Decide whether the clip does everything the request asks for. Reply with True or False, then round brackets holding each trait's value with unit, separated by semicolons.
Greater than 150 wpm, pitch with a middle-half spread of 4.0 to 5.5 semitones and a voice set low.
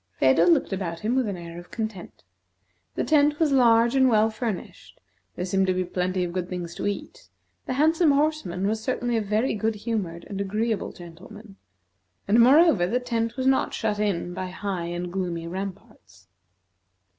False (180 wpm; 4.8 semitones; 205 Hz)